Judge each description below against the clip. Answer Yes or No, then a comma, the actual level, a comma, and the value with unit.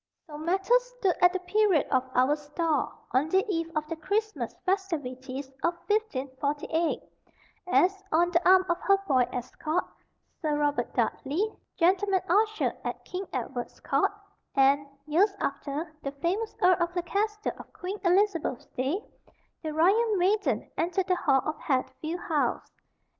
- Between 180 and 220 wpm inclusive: No, average, 145 wpm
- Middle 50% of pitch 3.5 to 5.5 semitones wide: Yes, average, 4.9 semitones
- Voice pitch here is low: No, very high, 340 Hz